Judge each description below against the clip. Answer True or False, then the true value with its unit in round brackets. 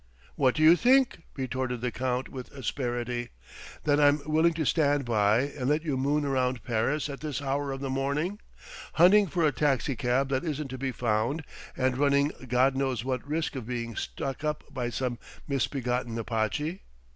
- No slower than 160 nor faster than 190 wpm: True (175 wpm)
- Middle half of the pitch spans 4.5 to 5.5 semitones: False (3.1 semitones)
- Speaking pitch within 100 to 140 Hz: True (135 Hz)